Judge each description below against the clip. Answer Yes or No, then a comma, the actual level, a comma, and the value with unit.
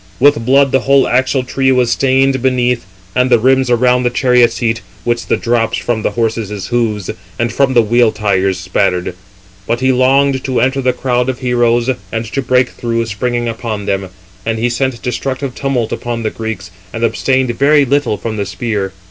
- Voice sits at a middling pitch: No, low, 120 Hz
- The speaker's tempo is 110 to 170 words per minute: No, average, 185 wpm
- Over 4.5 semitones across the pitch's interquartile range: No, narrow, 2.5 semitones